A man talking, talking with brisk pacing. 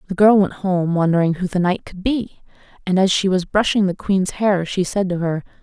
No: female; fast, 235 wpm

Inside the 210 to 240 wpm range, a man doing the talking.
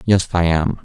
Yes: fast, 215 wpm; male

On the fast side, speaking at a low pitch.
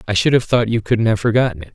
Yes: fast, 310 wpm; low, 110 Hz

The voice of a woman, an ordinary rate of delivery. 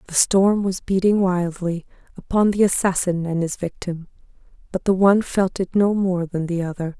Yes: female; average, 180 wpm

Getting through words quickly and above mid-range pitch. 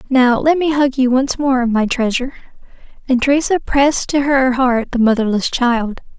No: average, 175 wpm; very high, 260 Hz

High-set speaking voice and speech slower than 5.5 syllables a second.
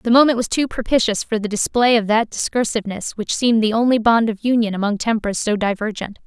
No: high, 225 Hz; 6.0 syllables/s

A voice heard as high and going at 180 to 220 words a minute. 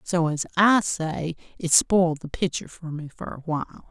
No: medium, 165 Hz; average, 200 wpm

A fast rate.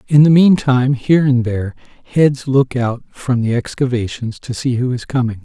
No: average, 190 wpm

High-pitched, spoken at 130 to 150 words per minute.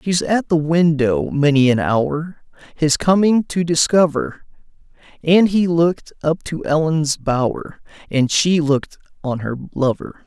No: medium, 155 Hz; average, 140 wpm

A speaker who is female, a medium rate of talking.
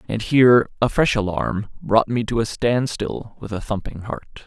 No: male; average, 190 wpm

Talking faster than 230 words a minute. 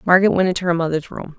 Yes: fast, 260 wpm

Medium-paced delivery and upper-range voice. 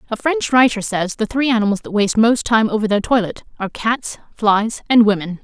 No: fast, 210 wpm; high, 220 Hz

